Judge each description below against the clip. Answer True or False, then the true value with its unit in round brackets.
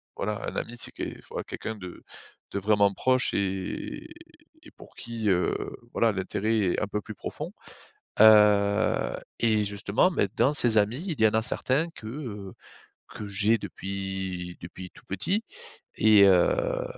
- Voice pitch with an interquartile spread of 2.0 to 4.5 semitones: True (2.9 semitones)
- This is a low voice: True (105 Hz)